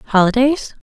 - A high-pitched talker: Yes, high, 240 Hz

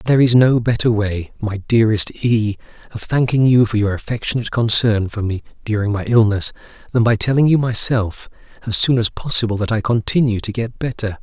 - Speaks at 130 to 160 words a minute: No, average, 185 wpm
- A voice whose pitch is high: No, low, 110 Hz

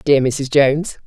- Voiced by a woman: Yes, female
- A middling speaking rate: Yes, average, 170 wpm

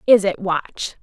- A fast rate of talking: No, average, 175 wpm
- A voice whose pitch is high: Yes, high, 195 Hz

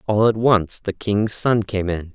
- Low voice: Yes, low, 105 Hz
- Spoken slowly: No, fast, 225 wpm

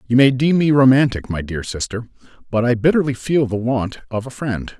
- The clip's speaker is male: Yes, male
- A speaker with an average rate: No, fast, 215 wpm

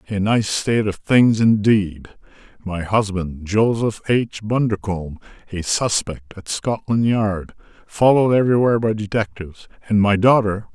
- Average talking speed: No, slow, 130 wpm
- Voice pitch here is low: Yes, low, 105 Hz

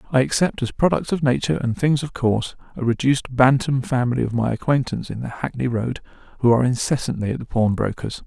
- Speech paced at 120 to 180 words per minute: No, average, 195 wpm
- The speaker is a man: Yes, male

